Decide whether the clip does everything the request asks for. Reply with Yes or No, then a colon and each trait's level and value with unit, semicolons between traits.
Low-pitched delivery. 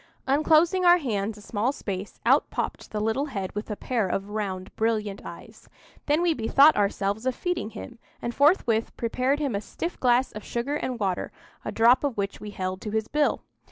No: high, 230 Hz